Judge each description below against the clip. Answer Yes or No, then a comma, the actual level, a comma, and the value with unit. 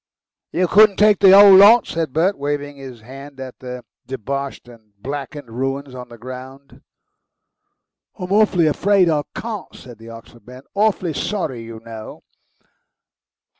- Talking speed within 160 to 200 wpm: No, average, 145 wpm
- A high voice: No, medium, 140 Hz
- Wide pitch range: Yes, wide, 6.8 semitones